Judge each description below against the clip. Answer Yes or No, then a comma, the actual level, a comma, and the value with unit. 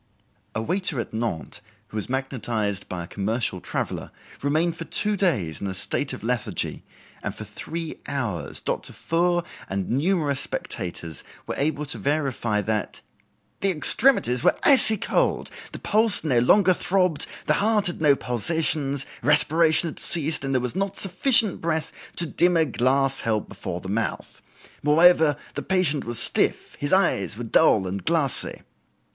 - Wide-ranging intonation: Yes, wide, 7.1 semitones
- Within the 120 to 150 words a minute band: No, average, 160 wpm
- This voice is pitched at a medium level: Yes, medium, 145 Hz